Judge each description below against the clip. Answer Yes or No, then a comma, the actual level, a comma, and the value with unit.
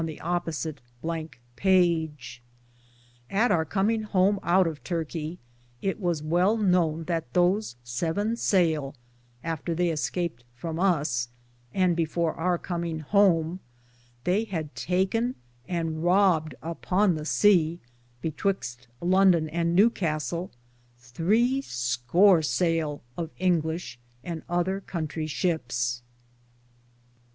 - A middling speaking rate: No, slow, 110 wpm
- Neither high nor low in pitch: Yes, medium, 170 Hz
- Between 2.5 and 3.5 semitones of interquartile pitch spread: Yes, average, 3.1 semitones